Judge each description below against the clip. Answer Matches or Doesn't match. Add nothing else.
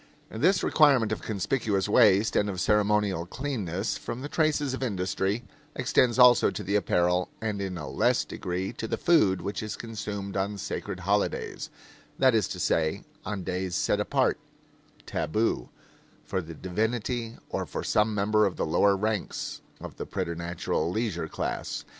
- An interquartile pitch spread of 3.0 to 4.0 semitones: Matches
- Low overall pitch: Matches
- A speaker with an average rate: Matches